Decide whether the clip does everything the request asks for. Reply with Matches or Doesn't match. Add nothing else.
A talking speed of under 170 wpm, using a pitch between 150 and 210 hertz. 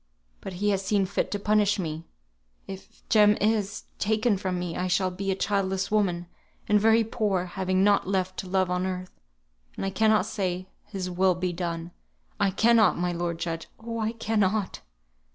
Doesn't match